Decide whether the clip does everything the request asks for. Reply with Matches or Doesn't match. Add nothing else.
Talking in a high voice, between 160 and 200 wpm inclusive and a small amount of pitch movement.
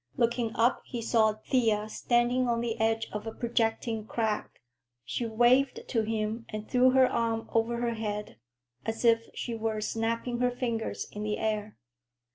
Matches